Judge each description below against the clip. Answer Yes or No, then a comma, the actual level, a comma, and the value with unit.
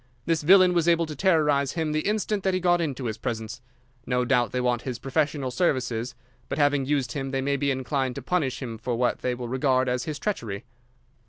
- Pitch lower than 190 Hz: Yes, low, 135 Hz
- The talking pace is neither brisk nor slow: No, fast, 220 wpm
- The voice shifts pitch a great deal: No, average, 4.0 semitones